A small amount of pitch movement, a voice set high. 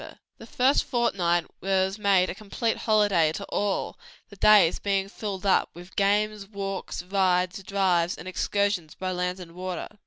Yes: narrow, 2.0 semitones; high, 195 Hz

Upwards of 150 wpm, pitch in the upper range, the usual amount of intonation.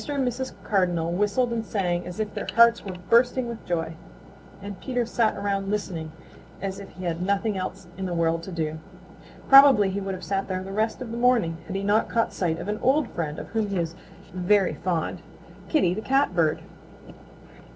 Yes: average, 200 wpm; high, 195 Hz; average, 4.4 semitones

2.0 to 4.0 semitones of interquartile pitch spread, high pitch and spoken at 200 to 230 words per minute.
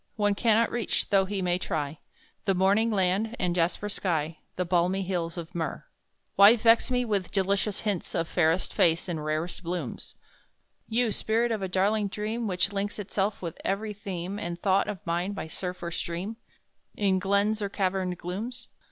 No: average, 3.0 semitones; high, 195 Hz; average, 175 wpm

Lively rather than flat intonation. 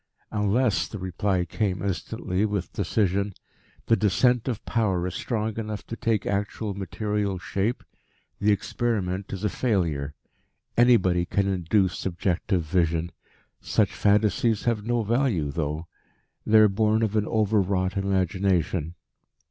No: average, 2.9 semitones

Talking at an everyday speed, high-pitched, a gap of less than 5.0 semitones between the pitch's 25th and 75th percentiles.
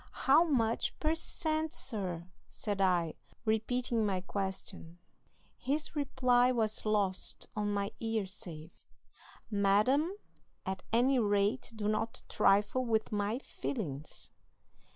No: slow, 110 wpm; high, 215 Hz; average, 4.4 semitones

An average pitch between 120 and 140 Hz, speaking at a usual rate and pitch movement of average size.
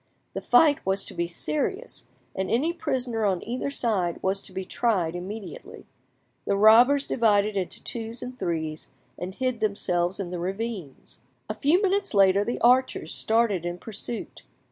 No: high, 215 Hz; average, 160 wpm; average, 4.9 semitones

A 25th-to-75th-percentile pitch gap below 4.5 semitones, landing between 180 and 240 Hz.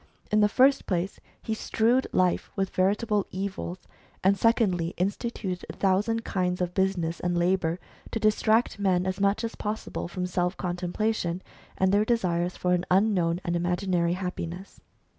Yes: average, 2.8 semitones; medium, 185 Hz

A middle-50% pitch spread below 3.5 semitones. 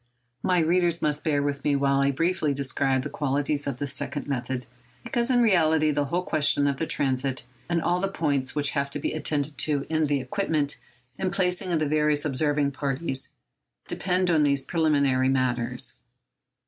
Yes: average, 2.9 semitones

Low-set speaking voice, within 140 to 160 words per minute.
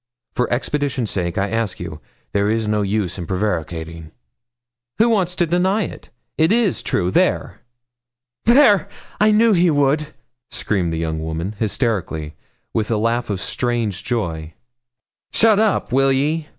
Yes: low, 115 Hz; average, 150 wpm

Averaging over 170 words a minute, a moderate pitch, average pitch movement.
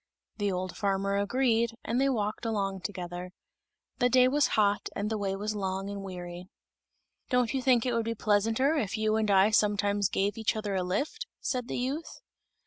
No: average, 190 wpm; high, 210 Hz; average, 3.5 semitones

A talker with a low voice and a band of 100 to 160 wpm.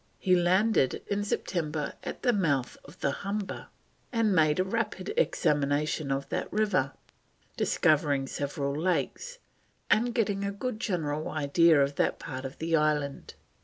No: medium, 165 Hz; average, 145 wpm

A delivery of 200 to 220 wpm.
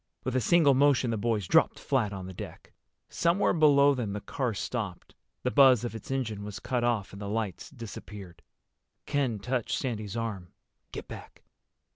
No: average, 175 wpm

